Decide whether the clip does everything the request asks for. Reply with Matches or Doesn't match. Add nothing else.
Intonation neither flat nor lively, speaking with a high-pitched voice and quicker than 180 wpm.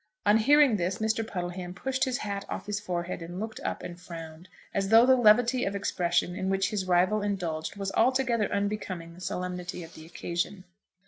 Matches